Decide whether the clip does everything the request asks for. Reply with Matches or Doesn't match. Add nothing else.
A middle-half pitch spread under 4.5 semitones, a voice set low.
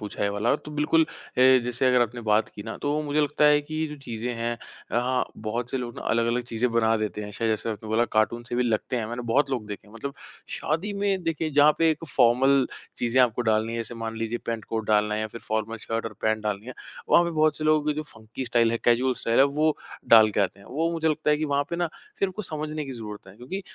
Doesn't match